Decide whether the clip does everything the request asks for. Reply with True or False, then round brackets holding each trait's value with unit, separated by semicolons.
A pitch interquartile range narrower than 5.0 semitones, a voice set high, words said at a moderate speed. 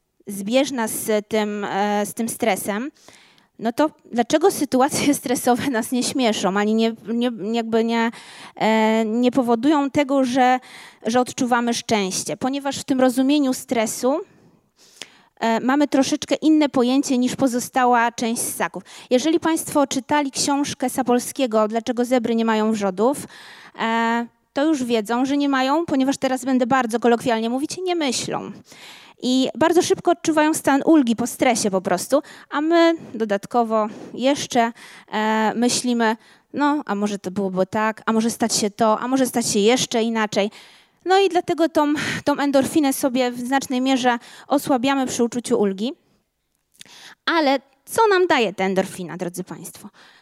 True (3.8 semitones; 250 Hz; 140 wpm)